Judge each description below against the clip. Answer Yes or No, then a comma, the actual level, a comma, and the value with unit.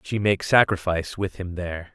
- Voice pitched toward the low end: Yes, very low, 95 Hz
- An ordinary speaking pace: Yes, average, 185 wpm